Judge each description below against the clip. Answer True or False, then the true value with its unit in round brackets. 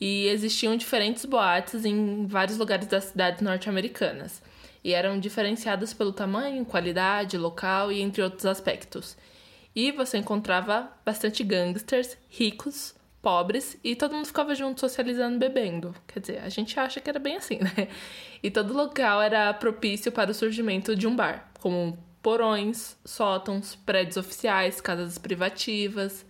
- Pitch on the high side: True (210 Hz)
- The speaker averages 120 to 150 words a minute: True (145 wpm)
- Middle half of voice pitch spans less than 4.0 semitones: True (3.2 semitones)